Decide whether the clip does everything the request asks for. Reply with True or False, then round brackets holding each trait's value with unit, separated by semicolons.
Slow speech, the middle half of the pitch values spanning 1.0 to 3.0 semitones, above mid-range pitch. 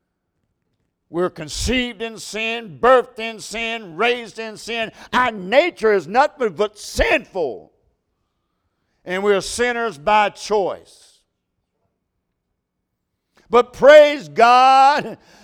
True (95 wpm; 2.6 semitones; 225 Hz)